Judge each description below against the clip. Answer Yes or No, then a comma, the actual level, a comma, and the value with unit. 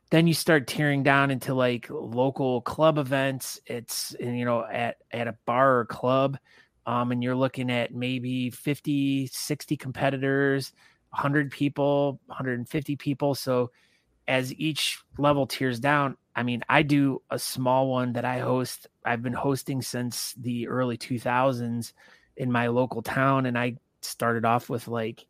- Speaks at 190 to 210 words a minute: No, average, 155 wpm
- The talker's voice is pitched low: Yes, low, 130 Hz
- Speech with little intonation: Yes, narrow, 2.2 semitones